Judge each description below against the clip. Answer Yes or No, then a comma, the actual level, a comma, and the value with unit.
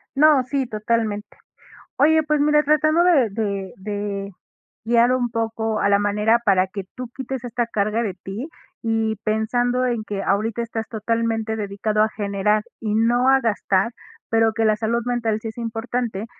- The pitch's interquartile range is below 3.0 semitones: Yes, narrow, 2.5 semitones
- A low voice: No, high, 225 Hz